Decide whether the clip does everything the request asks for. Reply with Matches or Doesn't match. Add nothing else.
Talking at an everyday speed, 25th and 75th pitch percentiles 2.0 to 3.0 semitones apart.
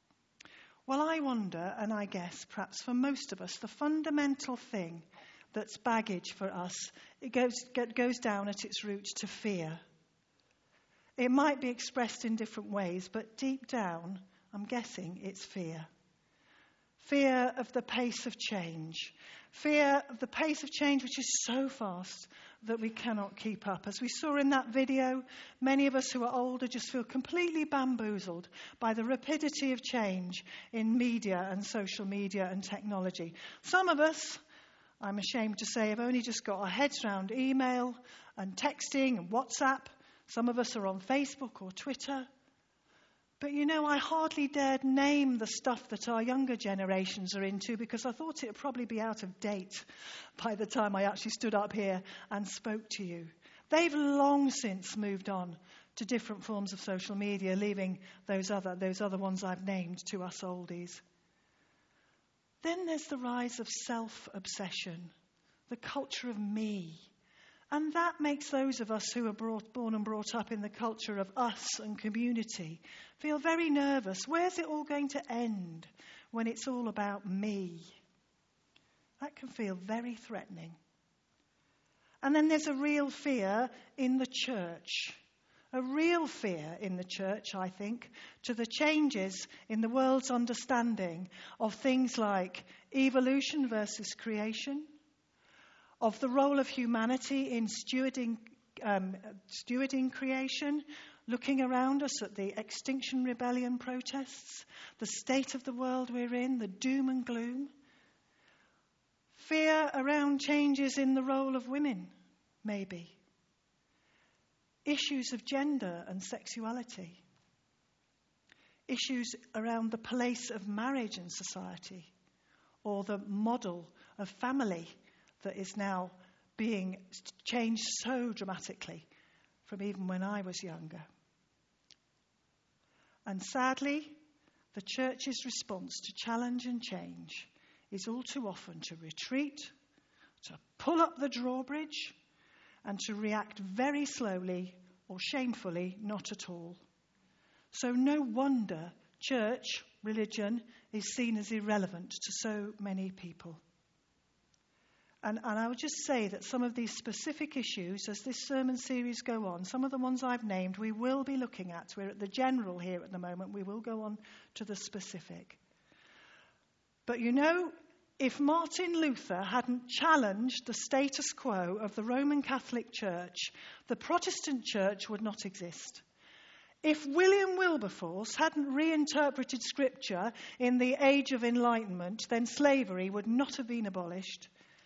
Doesn't match